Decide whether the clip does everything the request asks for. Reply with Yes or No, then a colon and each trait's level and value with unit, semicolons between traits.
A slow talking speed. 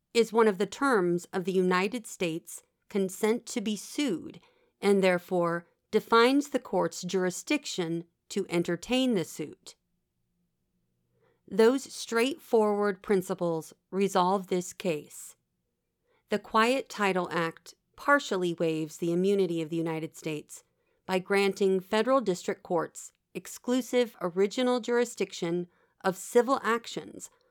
Yes: slow, 115 wpm